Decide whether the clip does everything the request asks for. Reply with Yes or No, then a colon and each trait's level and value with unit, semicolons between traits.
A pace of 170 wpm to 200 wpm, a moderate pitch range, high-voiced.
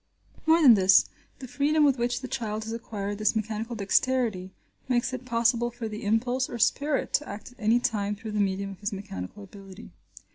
Yes: average, 195 wpm; average, 3.4 semitones; high, 225 Hz